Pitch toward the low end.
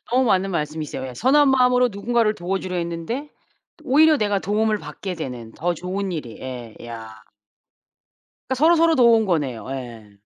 No: high, 190 Hz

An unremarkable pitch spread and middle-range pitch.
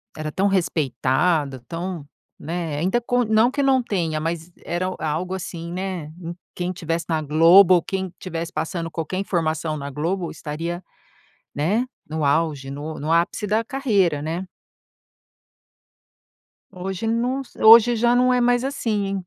Yes: average, 4.1 semitones; medium, 175 Hz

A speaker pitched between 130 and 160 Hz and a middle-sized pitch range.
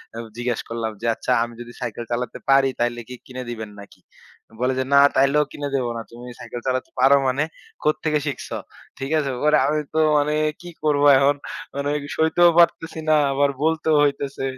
Yes: low, 135 Hz; average, 3.6 semitones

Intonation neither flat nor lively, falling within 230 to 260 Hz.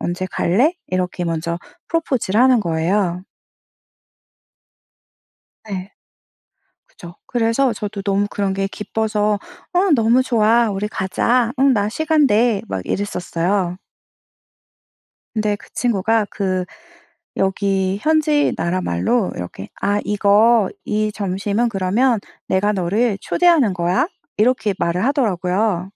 No: average, 4.0 semitones; high, 205 Hz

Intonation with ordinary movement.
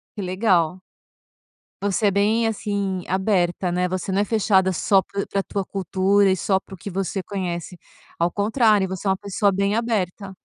No: narrow, 1.6 semitones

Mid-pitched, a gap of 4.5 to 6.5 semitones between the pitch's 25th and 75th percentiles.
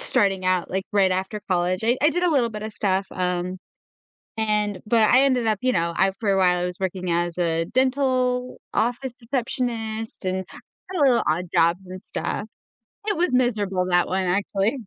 No: high, 205 Hz; average, 5.0 semitones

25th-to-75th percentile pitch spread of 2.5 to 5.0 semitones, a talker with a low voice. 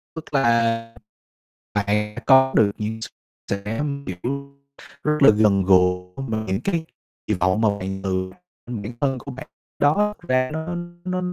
No: wide, 5.6 semitones; low, 115 Hz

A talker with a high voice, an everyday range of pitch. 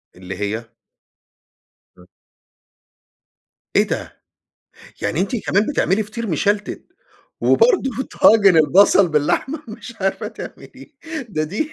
No: high, 200 Hz; wide, 7.1 semitones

